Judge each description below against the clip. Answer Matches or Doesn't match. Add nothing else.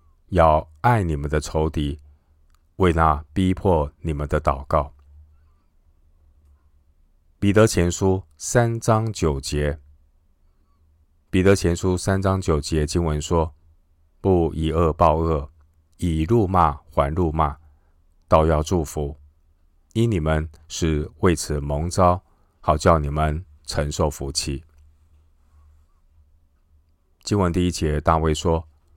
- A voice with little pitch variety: Matches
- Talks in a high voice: Doesn't match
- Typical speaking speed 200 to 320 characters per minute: Doesn't match